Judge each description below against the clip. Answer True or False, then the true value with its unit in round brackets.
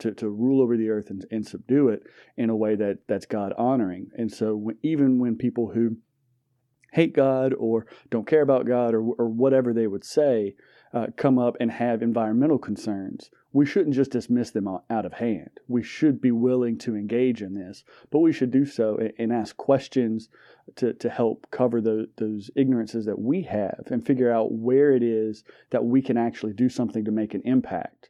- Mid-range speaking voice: False (120 Hz)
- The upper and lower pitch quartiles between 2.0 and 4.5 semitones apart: True (2.6 semitones)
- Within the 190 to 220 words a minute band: True (205 wpm)